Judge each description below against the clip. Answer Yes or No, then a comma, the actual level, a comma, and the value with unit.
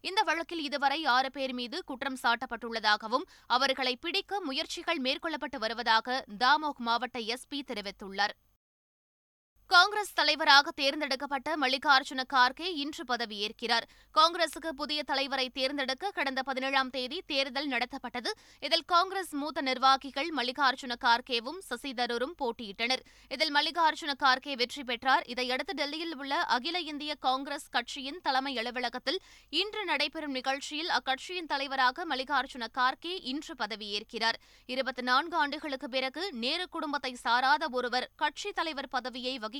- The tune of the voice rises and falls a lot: No, average, 3.4 semitones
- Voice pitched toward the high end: Yes, very high, 275 Hz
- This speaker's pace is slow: No, average, 110 wpm